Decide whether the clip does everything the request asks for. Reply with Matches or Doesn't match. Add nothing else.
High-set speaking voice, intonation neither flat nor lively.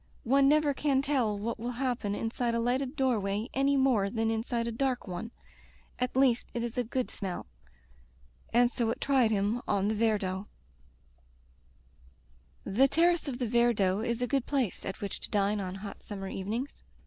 Matches